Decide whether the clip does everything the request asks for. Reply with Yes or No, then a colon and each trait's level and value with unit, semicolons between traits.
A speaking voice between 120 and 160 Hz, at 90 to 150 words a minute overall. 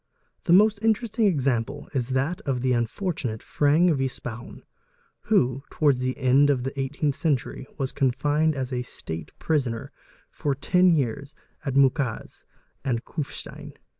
Yes: medium, 140 Hz; average, 145 wpm